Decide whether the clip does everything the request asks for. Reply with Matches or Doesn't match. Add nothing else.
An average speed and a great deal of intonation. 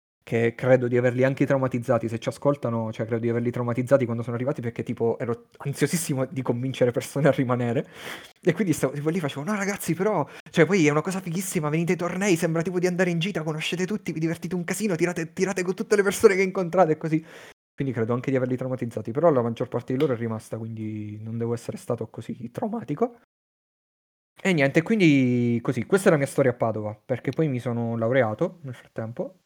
Doesn't match